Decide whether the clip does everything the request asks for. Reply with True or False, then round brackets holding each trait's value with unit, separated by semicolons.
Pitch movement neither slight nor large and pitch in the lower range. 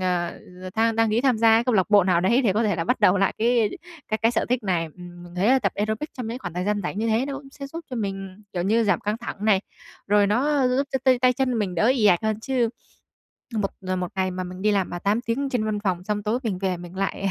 False (4.0 semitones; 210 Hz)